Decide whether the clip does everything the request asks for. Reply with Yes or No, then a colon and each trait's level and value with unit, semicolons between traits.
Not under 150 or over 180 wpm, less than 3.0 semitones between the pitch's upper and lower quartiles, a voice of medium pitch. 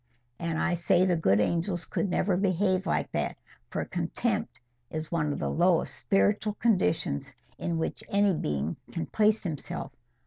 No: average, 160 wpm; average, 3.5 semitones; medium, 175 Hz